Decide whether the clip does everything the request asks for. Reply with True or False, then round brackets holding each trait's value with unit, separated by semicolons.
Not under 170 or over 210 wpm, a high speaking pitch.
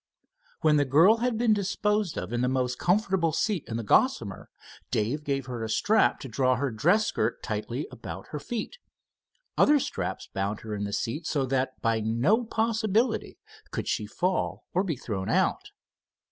False (175 wpm; 145 Hz)